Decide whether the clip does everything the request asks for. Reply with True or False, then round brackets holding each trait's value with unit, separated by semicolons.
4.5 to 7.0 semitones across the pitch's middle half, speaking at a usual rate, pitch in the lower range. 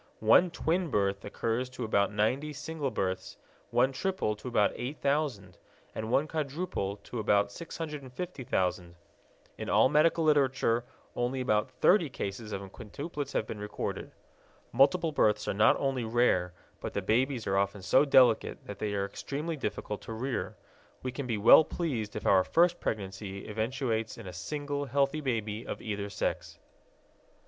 True (5.6 semitones; 155 wpm; 120 Hz)